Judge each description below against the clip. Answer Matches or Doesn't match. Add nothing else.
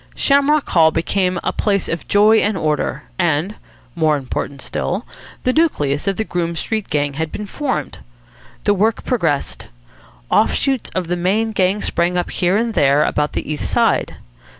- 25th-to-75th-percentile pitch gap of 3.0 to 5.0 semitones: Doesn't match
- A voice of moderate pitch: Matches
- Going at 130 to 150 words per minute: Doesn't match